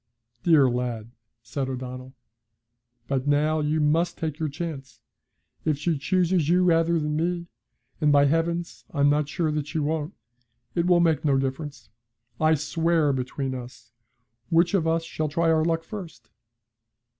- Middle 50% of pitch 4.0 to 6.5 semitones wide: No, average, 3.0 semitones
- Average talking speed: Yes, average, 155 wpm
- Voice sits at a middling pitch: Yes, medium, 155 Hz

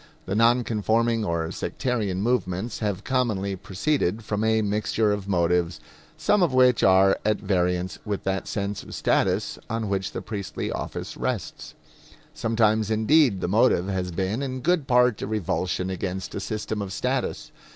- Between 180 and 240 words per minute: No, average, 160 wpm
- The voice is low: Yes, low, 105 Hz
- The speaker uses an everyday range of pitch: Yes, average, 3.4 semitones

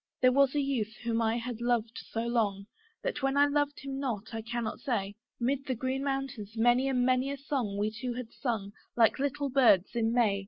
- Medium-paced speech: No, fast, 210 wpm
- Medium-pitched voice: No, high, 245 Hz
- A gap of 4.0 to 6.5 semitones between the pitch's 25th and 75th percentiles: No, average, 3.3 semitones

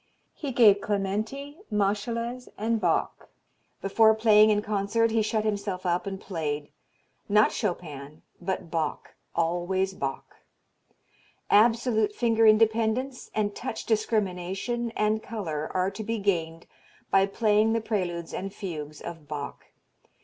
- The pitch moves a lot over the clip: No, average, 3.7 semitones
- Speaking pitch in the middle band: No, high, 205 Hz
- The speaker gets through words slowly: Yes, slow, 125 wpm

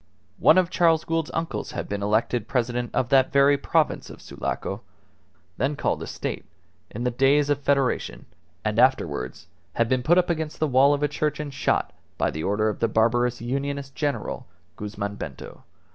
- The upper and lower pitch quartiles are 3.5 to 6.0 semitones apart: Yes, average, 4.1 semitones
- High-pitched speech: No, low, 135 Hz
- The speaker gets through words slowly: No, average, 185 wpm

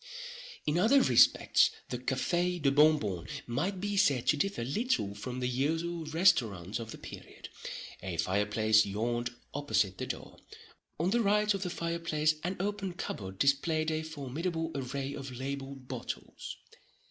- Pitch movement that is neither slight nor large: No, wide, 6.3 semitones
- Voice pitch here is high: No, medium, 145 Hz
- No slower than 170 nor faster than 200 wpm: No, average, 150 wpm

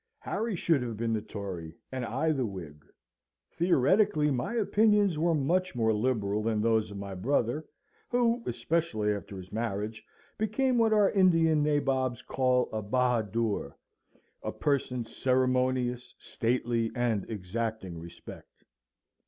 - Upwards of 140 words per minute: No, slow, 135 wpm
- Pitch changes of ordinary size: No, wide, 6.5 semitones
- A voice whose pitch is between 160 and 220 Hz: No, low, 125 Hz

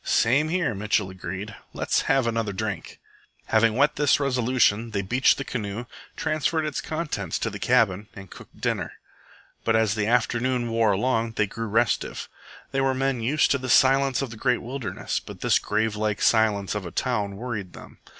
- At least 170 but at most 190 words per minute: Yes, average, 180 wpm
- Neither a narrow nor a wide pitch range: Yes, average, 3.8 semitones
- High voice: No, low, 115 Hz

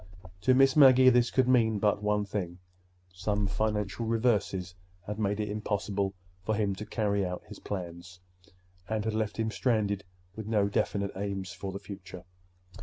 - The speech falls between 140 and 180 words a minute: Yes, average, 165 wpm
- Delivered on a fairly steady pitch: Yes, narrow, 2.0 semitones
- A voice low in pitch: Yes, low, 105 Hz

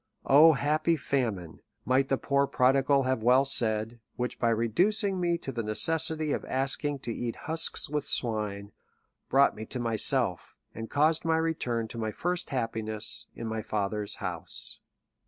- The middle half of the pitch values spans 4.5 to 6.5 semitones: Yes, average, 5.0 semitones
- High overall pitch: No, low, 130 Hz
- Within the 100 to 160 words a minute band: Yes, average, 155 wpm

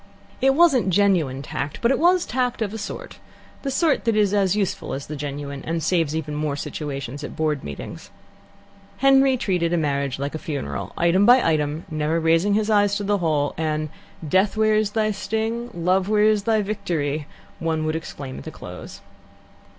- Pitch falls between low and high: Yes, medium, 180 Hz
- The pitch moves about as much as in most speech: No, wide, 6.0 semitones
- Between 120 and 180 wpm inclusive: No, average, 190 wpm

